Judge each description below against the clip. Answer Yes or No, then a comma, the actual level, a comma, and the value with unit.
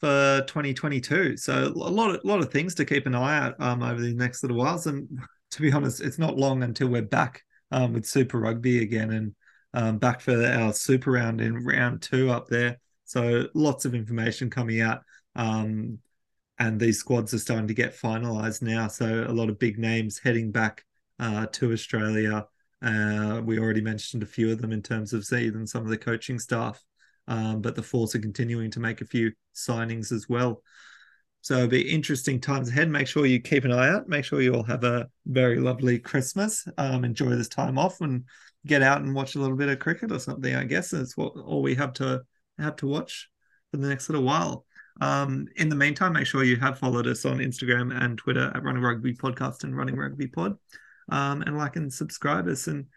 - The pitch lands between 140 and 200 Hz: No, low, 125 Hz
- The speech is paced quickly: Yes, fast, 215 wpm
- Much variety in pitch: No, average, 3.5 semitones